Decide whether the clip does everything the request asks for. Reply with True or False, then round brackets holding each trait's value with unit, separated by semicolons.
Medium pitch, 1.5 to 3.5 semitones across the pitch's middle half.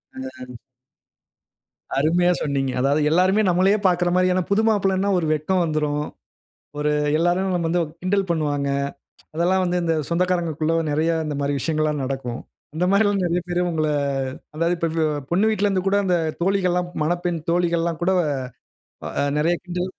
True (175 Hz; 3.1 semitones)